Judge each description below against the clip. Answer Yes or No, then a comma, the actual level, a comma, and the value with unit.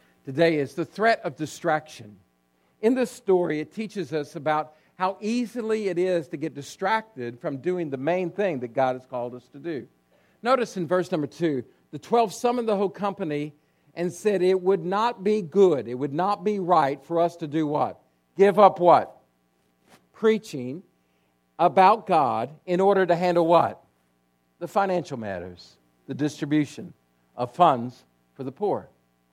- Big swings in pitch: Yes, wide, 7.4 semitones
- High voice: No, medium, 160 Hz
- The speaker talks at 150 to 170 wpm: Yes, average, 165 wpm